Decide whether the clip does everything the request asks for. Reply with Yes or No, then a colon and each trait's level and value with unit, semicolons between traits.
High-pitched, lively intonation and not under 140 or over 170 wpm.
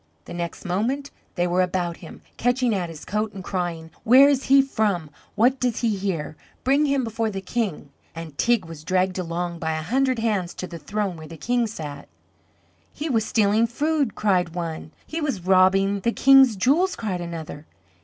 No: high, 195 Hz; wide, 5.8 semitones; average, 185 wpm